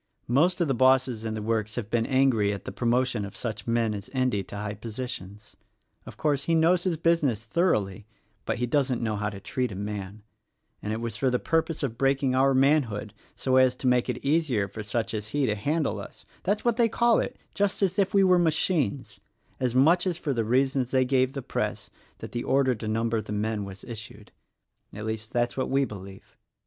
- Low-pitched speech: Yes, low, 125 Hz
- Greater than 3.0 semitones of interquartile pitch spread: Yes, average, 4.6 semitones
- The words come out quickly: Yes, fast, 225 wpm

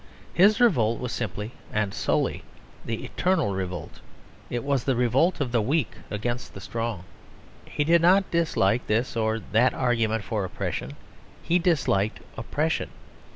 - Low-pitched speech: Yes, low, 120 Hz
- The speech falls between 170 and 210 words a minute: No, average, 145 wpm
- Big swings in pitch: Yes, wide, 5.7 semitones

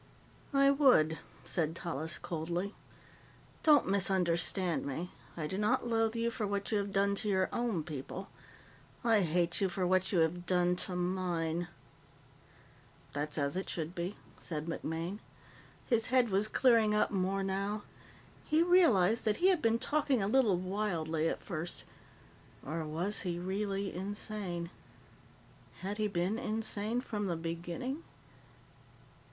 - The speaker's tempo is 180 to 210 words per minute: No, average, 145 wpm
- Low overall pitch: No, high, 190 Hz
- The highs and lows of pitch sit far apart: No, average, 3.9 semitones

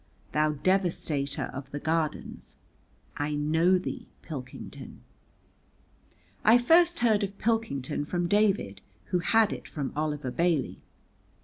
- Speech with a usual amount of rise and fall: No, wide, 5.8 semitones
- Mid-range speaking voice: Yes, medium, 165 Hz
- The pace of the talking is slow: Yes, slow, 115 wpm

